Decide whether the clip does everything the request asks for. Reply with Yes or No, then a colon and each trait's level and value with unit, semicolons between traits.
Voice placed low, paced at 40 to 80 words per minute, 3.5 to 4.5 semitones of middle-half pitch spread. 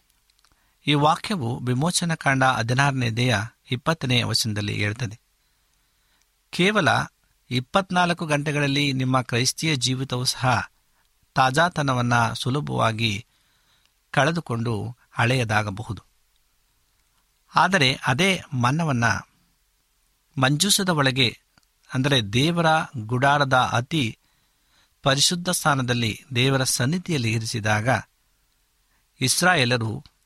Yes: low, 130 Hz; average, 70 wpm; average, 3.8 semitones